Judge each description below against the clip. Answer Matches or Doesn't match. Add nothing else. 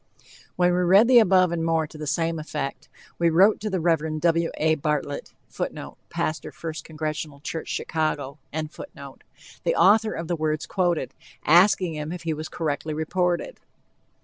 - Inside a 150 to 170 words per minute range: Matches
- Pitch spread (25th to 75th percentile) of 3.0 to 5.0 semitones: Doesn't match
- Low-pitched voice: Doesn't match